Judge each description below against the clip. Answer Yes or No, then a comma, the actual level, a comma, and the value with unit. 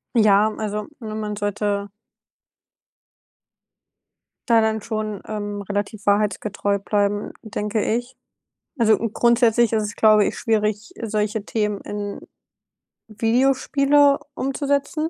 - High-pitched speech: Yes, high, 215 Hz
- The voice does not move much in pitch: Yes, narrow, 1.9 semitones